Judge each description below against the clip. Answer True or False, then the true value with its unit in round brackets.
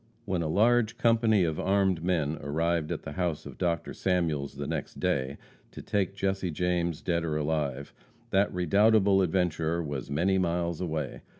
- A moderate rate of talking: True (165 wpm)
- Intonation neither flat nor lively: True (3.6 semitones)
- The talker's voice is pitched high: False (85 Hz)